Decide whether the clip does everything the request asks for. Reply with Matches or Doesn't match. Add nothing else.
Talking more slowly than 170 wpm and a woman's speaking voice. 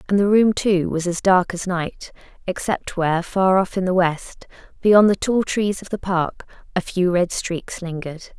Doesn't match